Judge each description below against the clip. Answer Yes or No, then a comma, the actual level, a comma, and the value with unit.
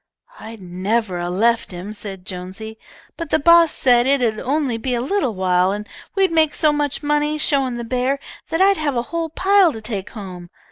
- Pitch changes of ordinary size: No, wide, 6.7 semitones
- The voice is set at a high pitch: Yes, high, 240 Hz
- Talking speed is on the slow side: No, average, 200 wpm